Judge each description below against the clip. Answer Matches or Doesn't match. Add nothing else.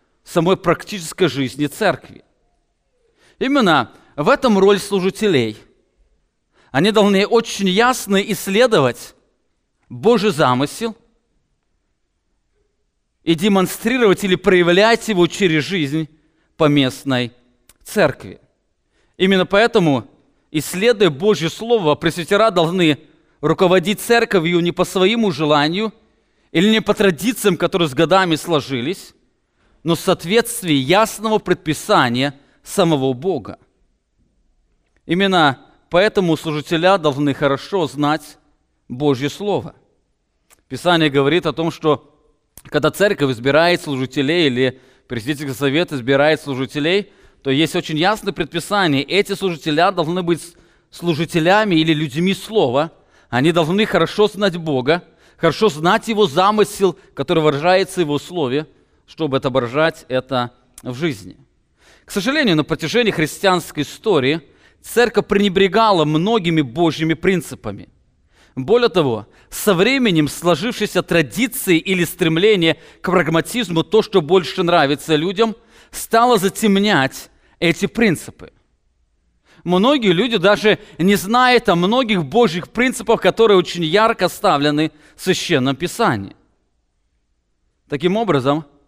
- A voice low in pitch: Doesn't match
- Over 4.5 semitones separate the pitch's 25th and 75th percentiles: Matches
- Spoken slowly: Matches